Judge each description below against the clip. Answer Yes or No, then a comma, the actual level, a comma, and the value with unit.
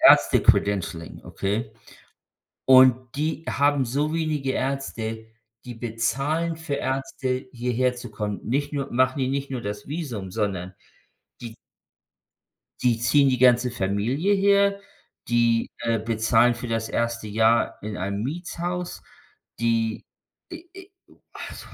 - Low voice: Yes, low, 125 Hz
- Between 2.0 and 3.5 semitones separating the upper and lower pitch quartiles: No, average, 3.9 semitones